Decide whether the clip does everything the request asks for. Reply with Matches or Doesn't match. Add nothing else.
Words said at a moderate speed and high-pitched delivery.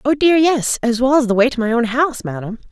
Doesn't match